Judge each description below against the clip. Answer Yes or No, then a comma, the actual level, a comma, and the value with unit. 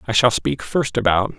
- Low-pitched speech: Yes, low, 120 Hz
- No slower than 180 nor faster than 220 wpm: Yes, fast, 215 wpm